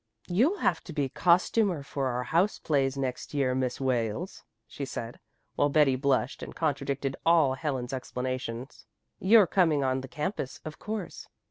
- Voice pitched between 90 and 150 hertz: Yes, medium, 140 Hz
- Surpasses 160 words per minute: No, average, 155 wpm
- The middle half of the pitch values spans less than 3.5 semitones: No, average, 4.2 semitones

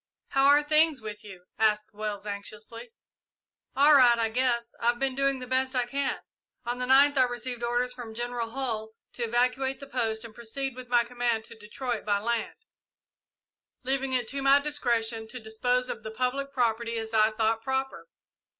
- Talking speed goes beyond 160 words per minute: Yes, average, 180 wpm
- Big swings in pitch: No, average, 3.0 semitones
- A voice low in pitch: No, high, 240 Hz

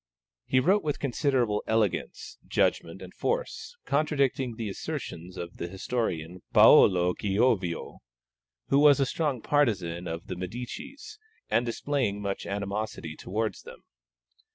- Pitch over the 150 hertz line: No, low, 110 Hz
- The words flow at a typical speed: No, slow, 125 wpm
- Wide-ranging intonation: Yes, wide, 7.2 semitones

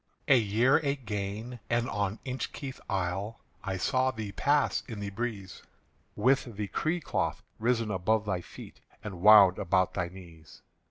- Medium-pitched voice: No, low, 105 Hz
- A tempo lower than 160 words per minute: Yes, average, 145 wpm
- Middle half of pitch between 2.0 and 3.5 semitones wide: No, average, 4.3 semitones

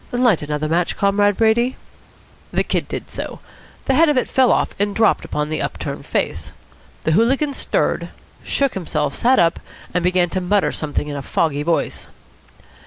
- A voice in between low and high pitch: No, high, 195 Hz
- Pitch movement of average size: No, wide, 7.2 semitones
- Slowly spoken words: No, average, 175 wpm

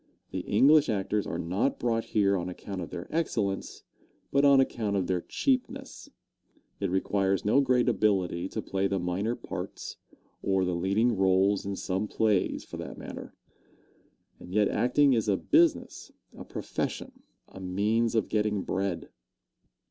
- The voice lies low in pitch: Yes, low, 100 Hz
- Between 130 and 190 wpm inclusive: Yes, average, 155 wpm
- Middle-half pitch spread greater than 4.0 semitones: No, average, 3.6 semitones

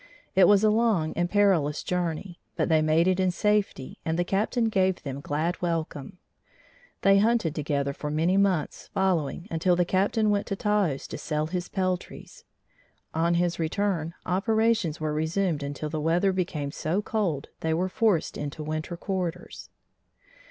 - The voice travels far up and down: No, average, 4.0 semitones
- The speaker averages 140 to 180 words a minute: Yes, average, 160 wpm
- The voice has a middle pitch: Yes, medium, 175 Hz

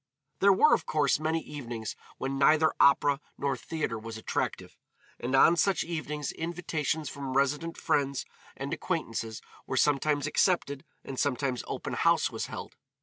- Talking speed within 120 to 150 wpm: Yes, average, 145 wpm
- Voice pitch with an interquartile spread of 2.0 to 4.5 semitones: Yes, average, 3.0 semitones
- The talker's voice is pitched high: No, medium, 145 Hz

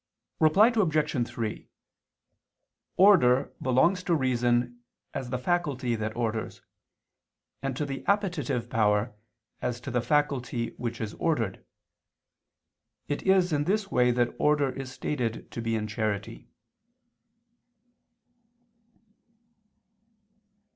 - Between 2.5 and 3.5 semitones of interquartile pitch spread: No, average, 4.6 semitones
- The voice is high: No, low, 125 Hz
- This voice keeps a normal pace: No, slow, 105 wpm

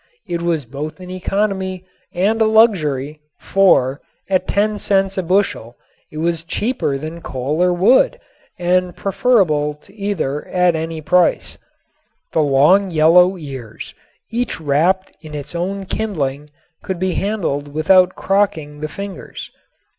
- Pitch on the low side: No, medium, 175 Hz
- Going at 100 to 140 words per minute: Yes, slow, 135 wpm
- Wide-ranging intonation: No, average, 4.5 semitones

